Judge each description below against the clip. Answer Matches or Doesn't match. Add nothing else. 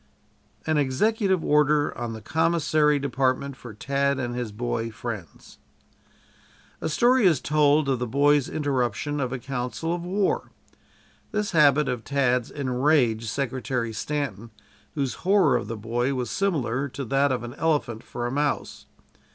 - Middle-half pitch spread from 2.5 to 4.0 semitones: Matches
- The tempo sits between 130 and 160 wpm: Matches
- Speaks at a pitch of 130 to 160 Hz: Matches